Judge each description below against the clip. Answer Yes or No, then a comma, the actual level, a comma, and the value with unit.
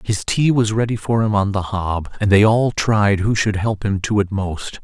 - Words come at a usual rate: No, fast, 250 wpm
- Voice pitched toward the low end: Yes, low, 105 Hz